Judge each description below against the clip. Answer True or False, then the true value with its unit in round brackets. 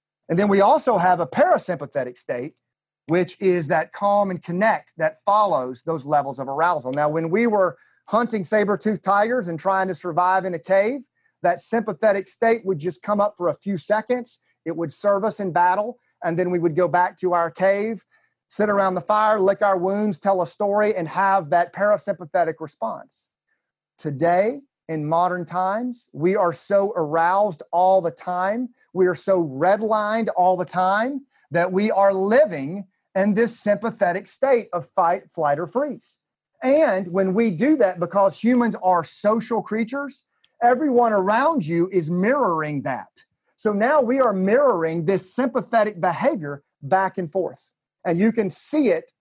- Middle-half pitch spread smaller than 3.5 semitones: False (3.8 semitones)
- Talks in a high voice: True (195 Hz)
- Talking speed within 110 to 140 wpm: False (170 wpm)